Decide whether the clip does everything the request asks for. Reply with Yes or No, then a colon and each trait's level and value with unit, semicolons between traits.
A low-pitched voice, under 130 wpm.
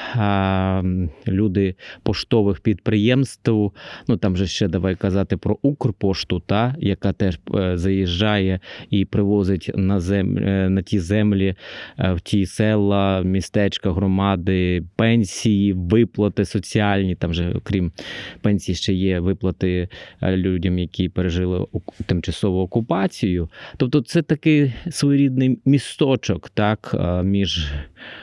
Yes: low, 100 Hz; slow, 105 wpm